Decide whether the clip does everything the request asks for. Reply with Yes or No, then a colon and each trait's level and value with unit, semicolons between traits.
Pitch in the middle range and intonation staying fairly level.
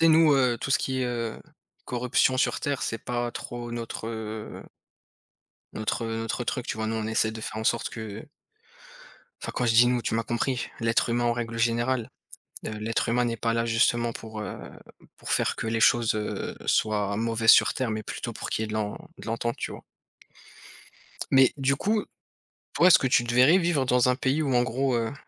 No: low, 120 Hz; narrow, 2.1 semitones